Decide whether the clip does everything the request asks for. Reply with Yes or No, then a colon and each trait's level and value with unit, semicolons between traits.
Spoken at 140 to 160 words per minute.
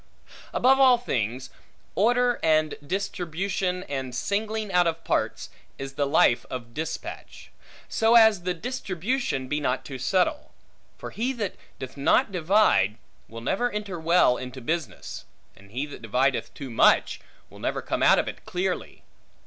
Yes: average, 150 wpm